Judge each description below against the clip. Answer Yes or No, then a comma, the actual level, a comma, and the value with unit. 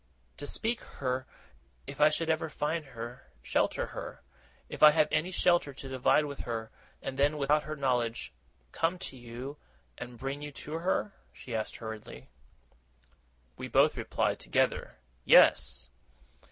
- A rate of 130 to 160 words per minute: Yes, average, 155 wpm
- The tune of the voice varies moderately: Yes, average, 3.8 semitones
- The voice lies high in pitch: No, medium, 140 Hz